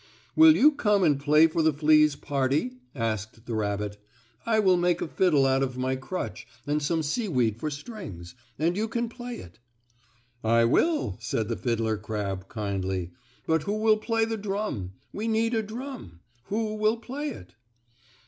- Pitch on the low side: No, medium, 155 Hz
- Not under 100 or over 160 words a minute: No, average, 170 wpm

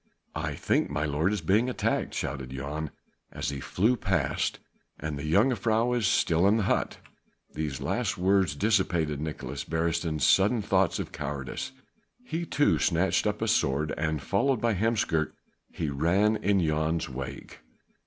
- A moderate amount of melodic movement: No, wide, 5.7 semitones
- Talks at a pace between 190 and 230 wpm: No, average, 155 wpm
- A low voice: Yes, very low, 85 Hz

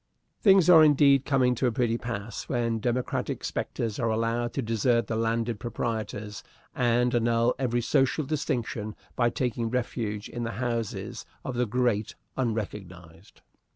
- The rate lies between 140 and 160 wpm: Yes, average, 145 wpm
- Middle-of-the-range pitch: No, low, 120 Hz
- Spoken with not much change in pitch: Yes, narrow, 2.0 semitones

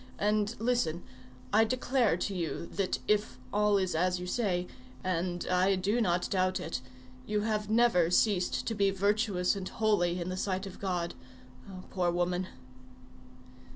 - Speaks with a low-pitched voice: No, medium, 185 Hz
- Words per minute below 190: Yes, average, 150 wpm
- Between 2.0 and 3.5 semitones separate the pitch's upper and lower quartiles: Yes, average, 2.9 semitones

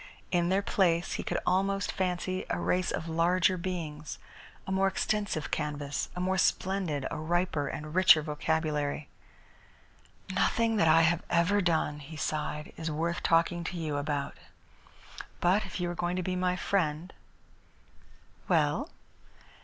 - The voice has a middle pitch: Yes, medium, 170 Hz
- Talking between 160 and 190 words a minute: No, average, 150 wpm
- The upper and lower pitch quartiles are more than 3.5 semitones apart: No, average, 3.1 semitones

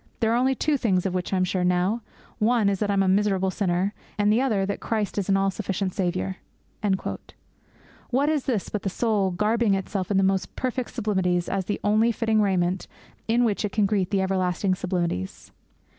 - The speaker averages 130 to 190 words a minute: No, fast, 205 wpm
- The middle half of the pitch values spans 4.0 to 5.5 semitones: No, average, 2.8 semitones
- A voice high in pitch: Yes, high, 195 Hz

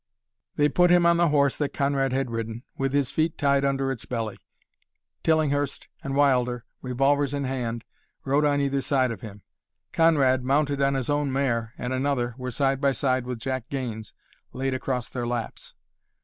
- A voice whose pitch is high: No, low, 135 Hz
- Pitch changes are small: Yes, narrow, 2.2 semitones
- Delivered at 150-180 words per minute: Yes, average, 175 wpm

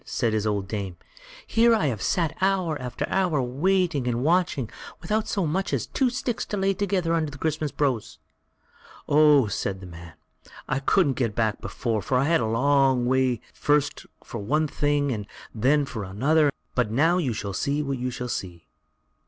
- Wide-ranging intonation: Yes, wide, 6.0 semitones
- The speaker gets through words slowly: No, average, 190 wpm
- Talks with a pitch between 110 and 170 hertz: Yes, medium, 140 Hz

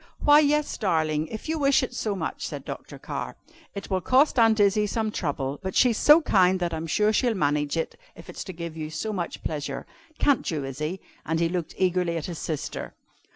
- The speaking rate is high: Yes, fast, 215 wpm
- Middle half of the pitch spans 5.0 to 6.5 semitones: Yes, wide, 5.6 semitones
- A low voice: No, medium, 185 Hz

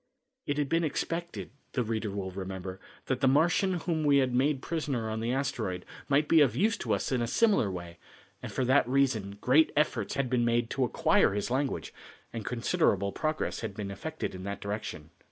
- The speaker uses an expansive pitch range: Yes, wide, 6.3 semitones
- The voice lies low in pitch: Yes, low, 125 Hz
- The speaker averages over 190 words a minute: Yes, average, 200 wpm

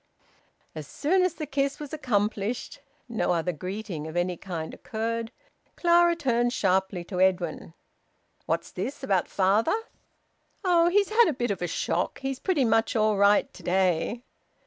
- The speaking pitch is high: Yes, high, 220 Hz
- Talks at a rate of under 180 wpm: Yes, average, 155 wpm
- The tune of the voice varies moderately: No, wide, 7.0 semitones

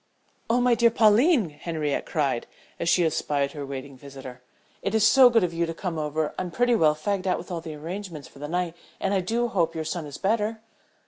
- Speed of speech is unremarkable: No, fast, 220 wpm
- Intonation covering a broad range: Yes, wide, 5.7 semitones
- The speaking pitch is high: No, medium, 170 Hz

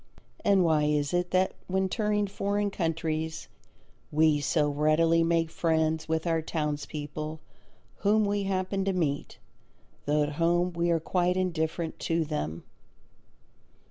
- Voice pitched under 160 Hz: No, medium, 165 Hz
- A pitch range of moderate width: Yes, average, 3.1 semitones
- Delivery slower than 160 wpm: Yes, slow, 135 wpm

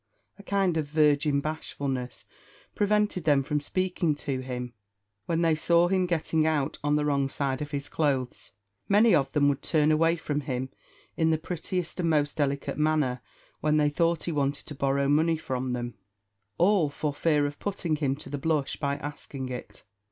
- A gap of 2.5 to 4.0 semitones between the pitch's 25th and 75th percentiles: Yes, average, 2.8 semitones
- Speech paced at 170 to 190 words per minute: Yes, average, 180 wpm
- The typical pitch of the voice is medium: Yes, medium, 150 Hz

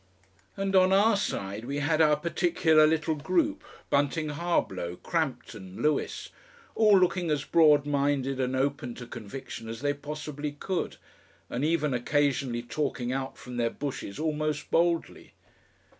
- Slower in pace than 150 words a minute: Yes, average, 140 wpm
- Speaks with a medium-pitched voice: Yes, medium, 145 Hz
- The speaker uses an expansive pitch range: No, average, 3.8 semitones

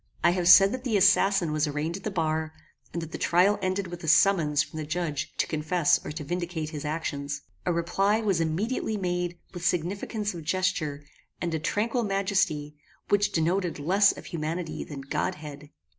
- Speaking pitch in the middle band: Yes, medium, 170 Hz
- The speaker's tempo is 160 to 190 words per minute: Yes, average, 185 wpm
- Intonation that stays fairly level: No, average, 3.9 semitones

